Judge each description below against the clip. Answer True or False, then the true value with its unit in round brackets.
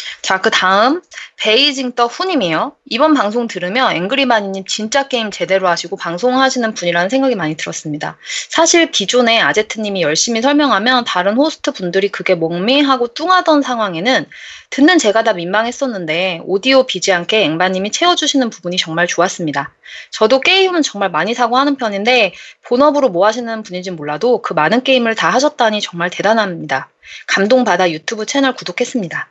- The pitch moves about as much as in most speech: False (6.3 semitones)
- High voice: True (225 Hz)